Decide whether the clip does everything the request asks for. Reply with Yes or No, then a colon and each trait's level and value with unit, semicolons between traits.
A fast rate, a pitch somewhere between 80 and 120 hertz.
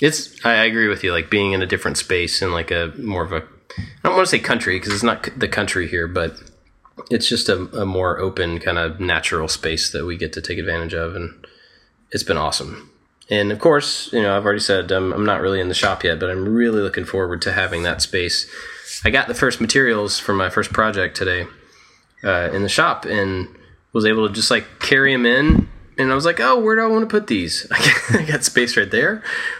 Yes: fast, 235 wpm; low, 105 Hz